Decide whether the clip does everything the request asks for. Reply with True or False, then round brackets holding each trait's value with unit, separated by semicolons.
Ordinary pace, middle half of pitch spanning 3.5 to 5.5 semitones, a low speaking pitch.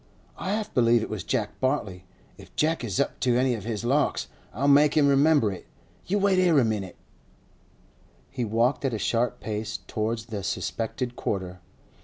True (180 wpm; 4.7 semitones; 120 Hz)